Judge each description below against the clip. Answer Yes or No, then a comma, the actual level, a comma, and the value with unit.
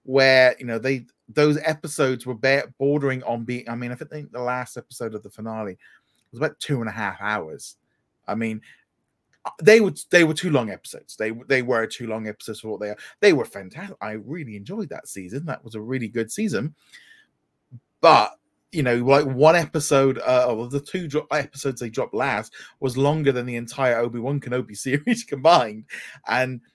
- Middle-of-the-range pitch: No, low, 130 Hz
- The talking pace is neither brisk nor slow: Yes, average, 195 wpm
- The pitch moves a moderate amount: Yes, average, 4.1 semitones